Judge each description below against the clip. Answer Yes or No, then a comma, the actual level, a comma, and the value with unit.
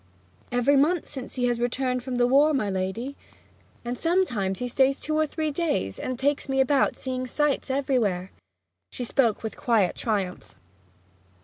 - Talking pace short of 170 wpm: Yes, average, 155 wpm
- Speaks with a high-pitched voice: Yes, very high, 255 Hz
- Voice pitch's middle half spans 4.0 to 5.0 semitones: No, average, 3.3 semitones